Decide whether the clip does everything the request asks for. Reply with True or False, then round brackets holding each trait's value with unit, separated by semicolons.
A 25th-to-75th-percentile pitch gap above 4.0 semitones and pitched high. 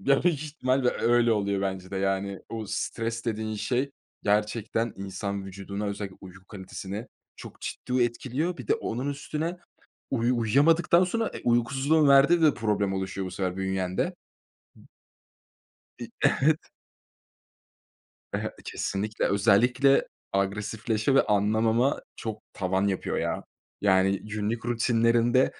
False (4.5 semitones; 110 Hz)